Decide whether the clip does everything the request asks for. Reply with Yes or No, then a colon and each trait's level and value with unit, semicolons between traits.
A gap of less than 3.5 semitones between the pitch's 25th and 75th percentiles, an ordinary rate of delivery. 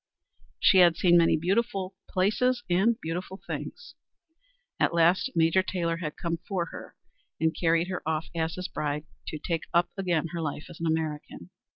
Yes: narrow, 2.4 semitones; average, 170 wpm